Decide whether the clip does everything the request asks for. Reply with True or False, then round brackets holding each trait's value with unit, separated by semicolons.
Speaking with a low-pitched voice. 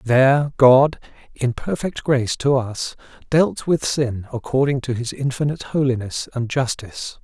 True (130 Hz)